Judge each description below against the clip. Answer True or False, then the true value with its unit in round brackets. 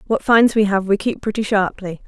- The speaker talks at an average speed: False (230 wpm)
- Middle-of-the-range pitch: False (205 Hz)